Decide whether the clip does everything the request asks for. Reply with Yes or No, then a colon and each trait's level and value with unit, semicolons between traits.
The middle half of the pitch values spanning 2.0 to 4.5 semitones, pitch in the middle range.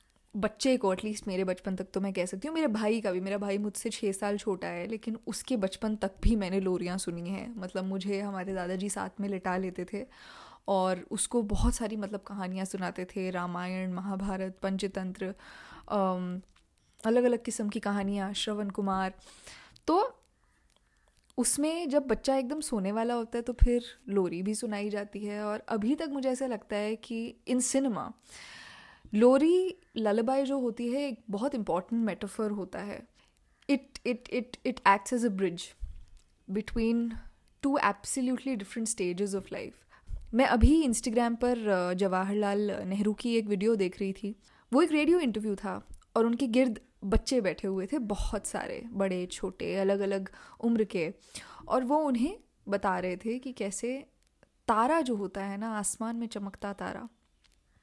No: average, 3.9 semitones; high, 210 Hz